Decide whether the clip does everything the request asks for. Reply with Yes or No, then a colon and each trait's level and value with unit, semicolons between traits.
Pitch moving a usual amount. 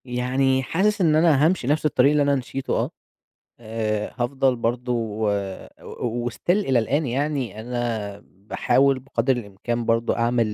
Yes: average, 3.2 semitones